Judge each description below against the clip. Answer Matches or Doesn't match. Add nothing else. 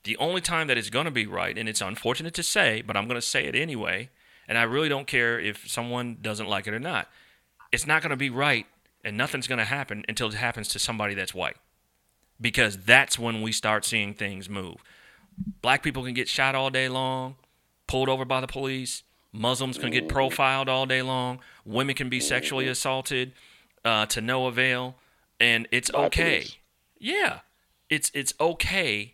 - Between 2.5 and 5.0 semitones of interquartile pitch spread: Matches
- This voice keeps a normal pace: Matches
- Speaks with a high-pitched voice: Doesn't match